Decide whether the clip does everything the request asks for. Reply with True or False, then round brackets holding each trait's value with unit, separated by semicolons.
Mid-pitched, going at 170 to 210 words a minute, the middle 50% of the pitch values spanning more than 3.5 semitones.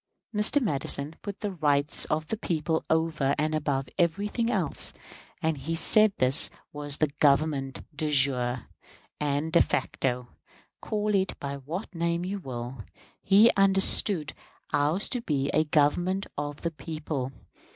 False (155 Hz; 140 wpm; 4.8 semitones)